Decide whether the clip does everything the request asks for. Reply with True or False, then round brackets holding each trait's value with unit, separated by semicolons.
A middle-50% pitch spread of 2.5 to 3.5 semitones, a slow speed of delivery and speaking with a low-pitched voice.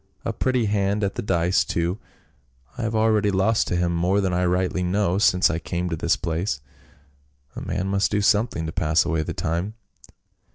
False (3.2 semitones; 200 wpm; 95 Hz)